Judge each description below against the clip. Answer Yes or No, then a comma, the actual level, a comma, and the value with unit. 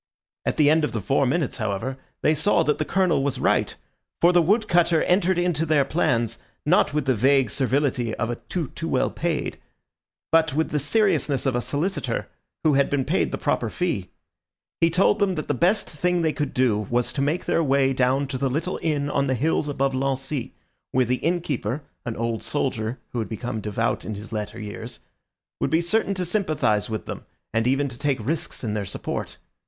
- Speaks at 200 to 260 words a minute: Yes, fast, 205 wpm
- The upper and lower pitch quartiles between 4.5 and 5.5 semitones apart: Yes, average, 5.0 semitones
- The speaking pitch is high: No, medium, 140 Hz